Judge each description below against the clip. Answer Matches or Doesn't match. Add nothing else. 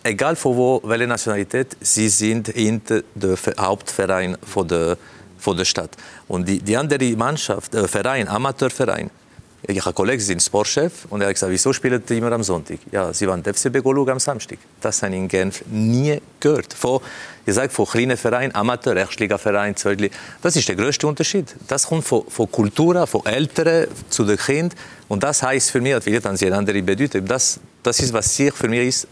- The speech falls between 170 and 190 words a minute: Matches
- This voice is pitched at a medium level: Doesn't match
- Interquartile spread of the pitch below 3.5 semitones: Doesn't match